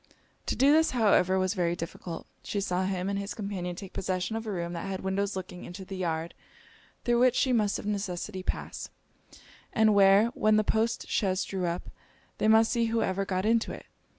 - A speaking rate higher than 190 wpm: Yes, average, 200 wpm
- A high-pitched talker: Yes, high, 195 Hz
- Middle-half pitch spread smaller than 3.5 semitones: Yes, average, 3.0 semitones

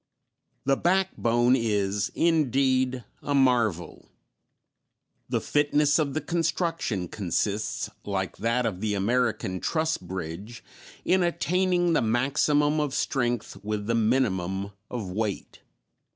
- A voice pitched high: No, low, 120 Hz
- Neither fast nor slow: No, slow, 110 wpm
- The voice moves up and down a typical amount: No, wide, 6.2 semitones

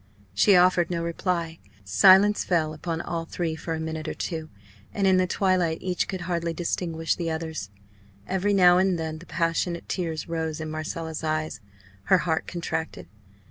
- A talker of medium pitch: Yes, medium, 165 Hz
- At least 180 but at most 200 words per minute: No, average, 170 wpm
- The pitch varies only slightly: Yes, narrow, 2.0 semitones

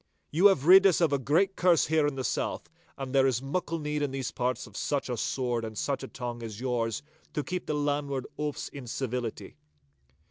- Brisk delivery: Yes, fast, 215 wpm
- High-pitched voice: No, low, 135 Hz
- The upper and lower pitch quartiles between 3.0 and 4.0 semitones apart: Yes, average, 3.3 semitones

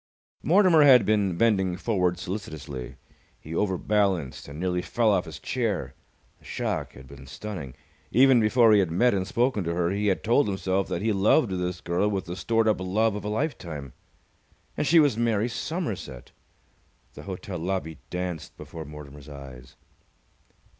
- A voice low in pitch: Yes, very low, 95 Hz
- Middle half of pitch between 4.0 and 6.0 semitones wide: Yes, average, 4.6 semitones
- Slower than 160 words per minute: No, average, 165 wpm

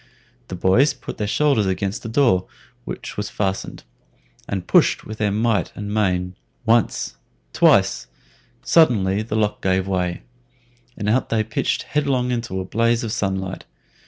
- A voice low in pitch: Yes, low, 105 Hz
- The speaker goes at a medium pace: Yes, average, 145 wpm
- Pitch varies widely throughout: No, average, 3.6 semitones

